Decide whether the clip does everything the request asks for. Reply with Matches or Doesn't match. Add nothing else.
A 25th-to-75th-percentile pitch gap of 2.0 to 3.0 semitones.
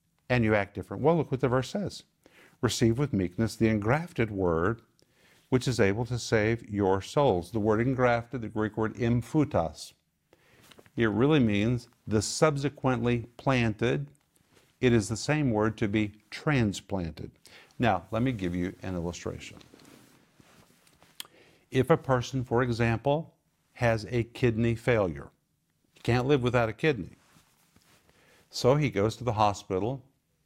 Doesn't match